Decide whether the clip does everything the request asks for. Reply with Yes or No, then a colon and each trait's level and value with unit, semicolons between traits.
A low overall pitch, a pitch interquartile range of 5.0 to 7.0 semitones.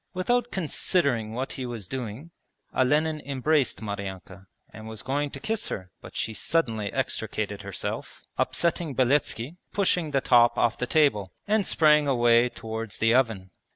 Yes: low, 130 Hz; wide, 5.4 semitones